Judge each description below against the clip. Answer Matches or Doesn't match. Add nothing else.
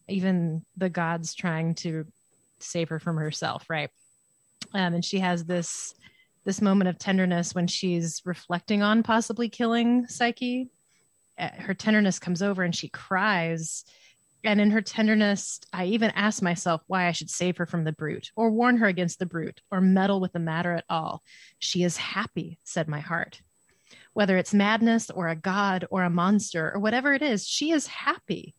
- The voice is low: Doesn't match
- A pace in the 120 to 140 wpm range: Doesn't match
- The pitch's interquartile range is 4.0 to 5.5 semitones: Doesn't match